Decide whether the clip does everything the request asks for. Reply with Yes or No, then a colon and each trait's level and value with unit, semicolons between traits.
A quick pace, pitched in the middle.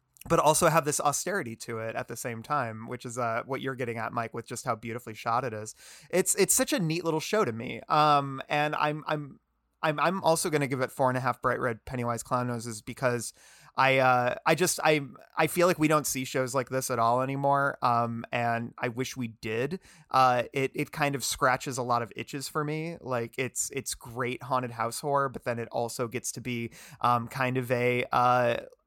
No: fast, 225 wpm; low, 130 Hz